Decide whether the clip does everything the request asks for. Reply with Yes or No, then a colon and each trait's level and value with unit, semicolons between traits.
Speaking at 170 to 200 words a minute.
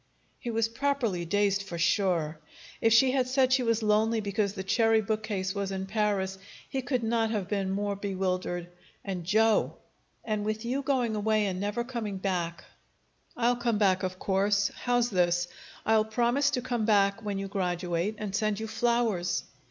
Yes: average, 175 wpm